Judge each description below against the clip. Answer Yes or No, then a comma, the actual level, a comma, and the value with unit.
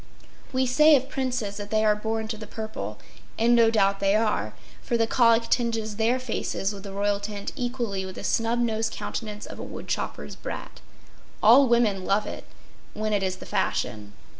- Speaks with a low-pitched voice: No, high, 220 Hz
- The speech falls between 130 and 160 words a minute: No, average, 185 wpm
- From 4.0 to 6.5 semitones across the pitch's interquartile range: No, average, 2.7 semitones